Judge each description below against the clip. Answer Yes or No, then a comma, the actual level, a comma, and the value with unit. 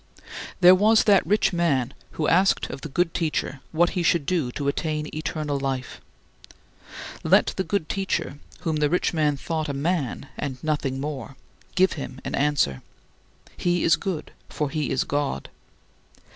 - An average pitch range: Yes, average, 3.8 semitones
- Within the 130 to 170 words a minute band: Yes, average, 160 wpm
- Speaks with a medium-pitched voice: Yes, medium, 155 Hz